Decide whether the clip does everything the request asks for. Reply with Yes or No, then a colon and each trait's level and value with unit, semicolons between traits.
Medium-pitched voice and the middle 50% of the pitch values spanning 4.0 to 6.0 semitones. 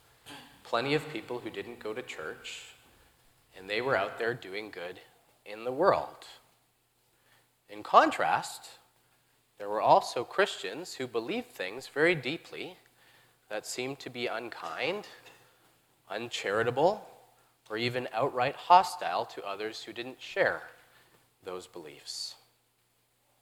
No: low, 120 Hz; average, 4.4 semitones